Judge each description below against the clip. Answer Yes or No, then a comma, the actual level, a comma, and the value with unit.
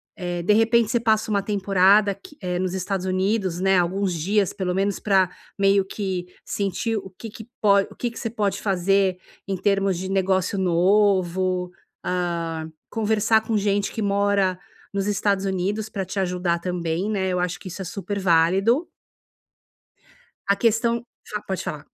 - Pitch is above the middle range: Yes, high, 195 Hz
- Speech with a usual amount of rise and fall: No, narrow, 2.2 semitones